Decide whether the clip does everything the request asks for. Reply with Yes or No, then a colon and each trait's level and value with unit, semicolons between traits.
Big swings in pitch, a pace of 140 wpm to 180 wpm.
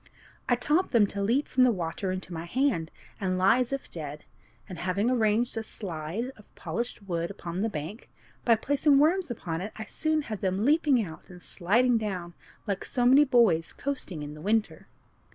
No: wide, 5.9 semitones; average, 190 wpm